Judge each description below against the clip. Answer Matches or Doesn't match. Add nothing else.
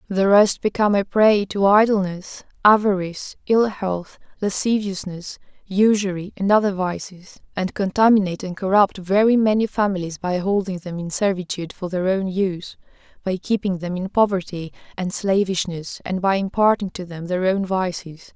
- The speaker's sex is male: Doesn't match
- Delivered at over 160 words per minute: Doesn't match